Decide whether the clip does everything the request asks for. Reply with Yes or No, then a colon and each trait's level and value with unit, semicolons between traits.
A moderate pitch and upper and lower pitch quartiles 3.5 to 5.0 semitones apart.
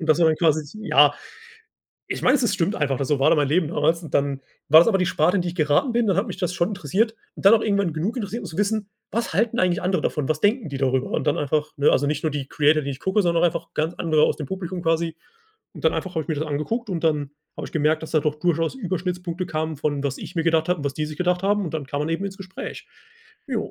Yes: medium, 165 Hz; average, 4.0 semitones